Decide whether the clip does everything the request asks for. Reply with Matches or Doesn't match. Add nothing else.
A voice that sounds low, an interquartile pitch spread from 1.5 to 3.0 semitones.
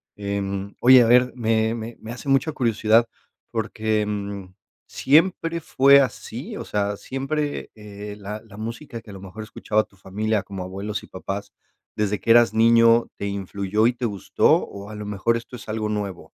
Matches